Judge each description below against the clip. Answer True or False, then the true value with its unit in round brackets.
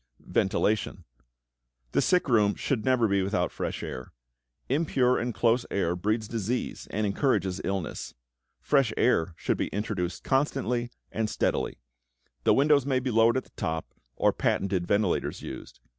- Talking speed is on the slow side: False (145 wpm)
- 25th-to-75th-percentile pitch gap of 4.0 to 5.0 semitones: True (4.5 semitones)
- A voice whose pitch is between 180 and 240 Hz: False (110 Hz)